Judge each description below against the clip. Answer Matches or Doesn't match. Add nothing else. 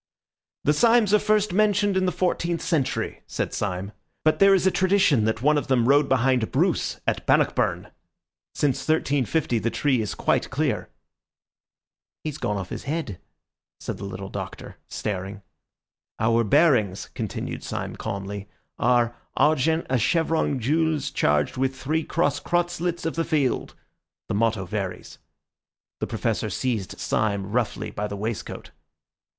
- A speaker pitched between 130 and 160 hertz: Matches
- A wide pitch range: Matches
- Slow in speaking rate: Doesn't match